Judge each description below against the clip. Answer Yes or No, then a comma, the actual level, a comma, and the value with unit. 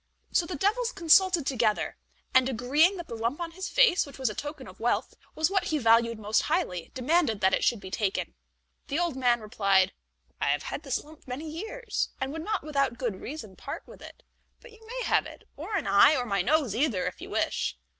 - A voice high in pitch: Yes, very high, 275 Hz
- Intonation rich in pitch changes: Yes, wide, 7.1 semitones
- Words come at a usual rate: No, fast, 220 wpm